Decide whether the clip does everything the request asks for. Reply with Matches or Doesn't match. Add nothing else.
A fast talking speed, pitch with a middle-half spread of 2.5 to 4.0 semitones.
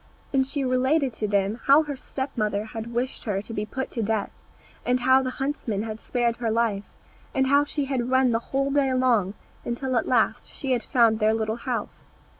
Matches